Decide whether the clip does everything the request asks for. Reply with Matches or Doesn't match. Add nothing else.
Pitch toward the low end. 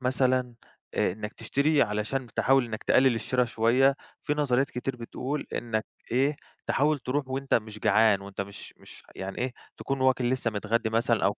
Matches